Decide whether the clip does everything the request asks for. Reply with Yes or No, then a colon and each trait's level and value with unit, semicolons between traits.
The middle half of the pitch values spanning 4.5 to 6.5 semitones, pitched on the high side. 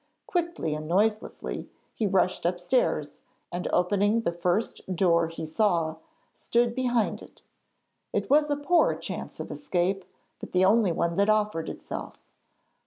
Yes: average, 5.1 semitones; high, 195 Hz